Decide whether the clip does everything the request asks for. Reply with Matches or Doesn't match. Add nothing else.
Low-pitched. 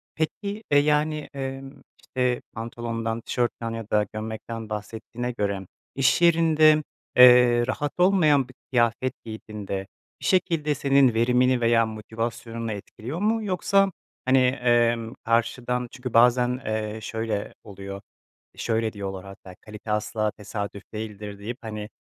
Matches